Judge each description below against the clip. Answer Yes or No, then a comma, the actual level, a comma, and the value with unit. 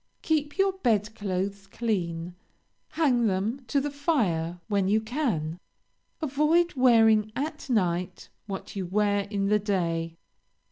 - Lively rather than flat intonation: Yes, wide, 6.2 semitones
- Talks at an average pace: No, slow, 130 wpm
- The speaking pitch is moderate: No, high, 210 Hz